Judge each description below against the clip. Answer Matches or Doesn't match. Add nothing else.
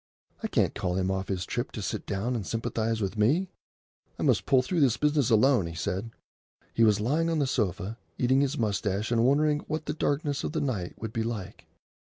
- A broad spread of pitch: Matches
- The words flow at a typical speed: Doesn't match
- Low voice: Matches